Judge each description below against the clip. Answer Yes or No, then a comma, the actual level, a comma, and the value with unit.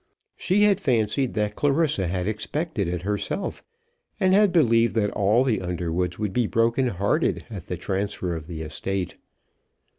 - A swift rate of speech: No, average, 155 wpm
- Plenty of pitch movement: Yes, wide, 6.2 semitones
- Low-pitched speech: Yes, low, 105 Hz